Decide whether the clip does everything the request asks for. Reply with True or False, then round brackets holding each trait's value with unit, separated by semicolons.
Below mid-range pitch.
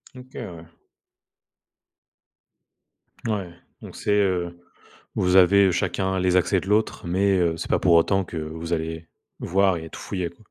True (90 Hz)